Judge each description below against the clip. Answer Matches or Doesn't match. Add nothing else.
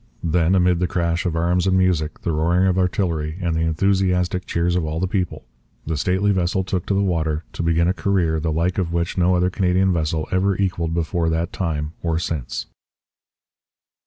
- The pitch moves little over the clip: Matches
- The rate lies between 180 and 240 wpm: Matches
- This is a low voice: Matches